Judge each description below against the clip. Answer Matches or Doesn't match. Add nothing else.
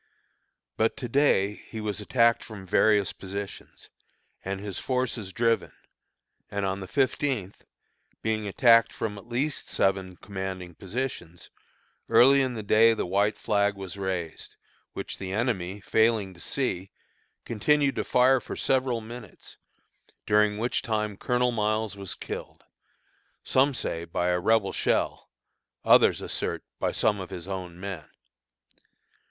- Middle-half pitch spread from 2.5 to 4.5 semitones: Matches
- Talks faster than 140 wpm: Doesn't match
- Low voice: Matches